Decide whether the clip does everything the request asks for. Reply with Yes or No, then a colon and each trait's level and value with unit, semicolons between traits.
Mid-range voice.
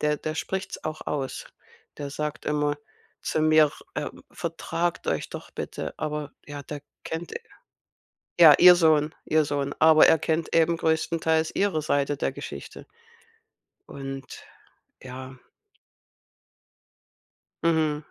Yes: medium, 155 Hz